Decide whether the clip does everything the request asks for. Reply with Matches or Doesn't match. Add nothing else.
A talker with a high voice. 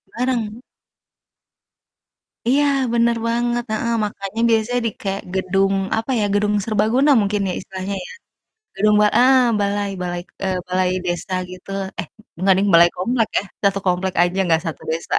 Matches